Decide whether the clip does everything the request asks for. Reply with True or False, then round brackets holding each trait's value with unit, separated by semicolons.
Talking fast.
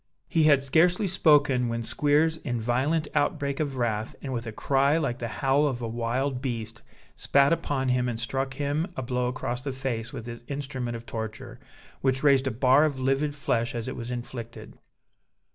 False (195 wpm)